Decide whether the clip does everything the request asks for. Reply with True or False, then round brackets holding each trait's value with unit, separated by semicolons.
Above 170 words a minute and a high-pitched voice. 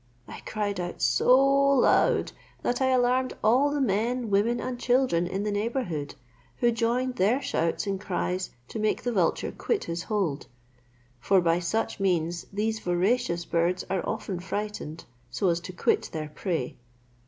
False (160 wpm; 205 Hz)